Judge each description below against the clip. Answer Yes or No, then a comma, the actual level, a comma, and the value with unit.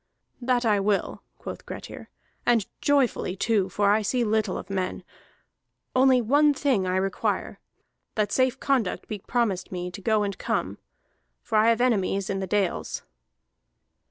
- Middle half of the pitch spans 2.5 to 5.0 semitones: Yes, average, 3.9 semitones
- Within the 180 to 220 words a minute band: No, average, 155 wpm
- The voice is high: Yes, high, 215 Hz